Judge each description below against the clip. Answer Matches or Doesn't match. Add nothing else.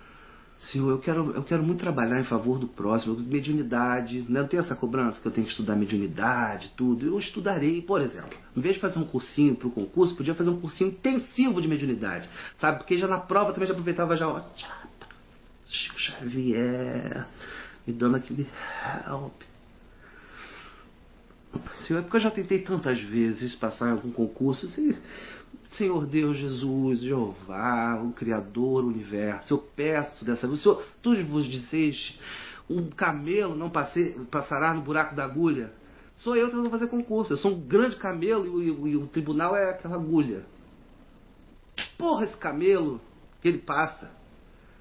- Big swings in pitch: Matches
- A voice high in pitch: Doesn't match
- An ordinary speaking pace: Matches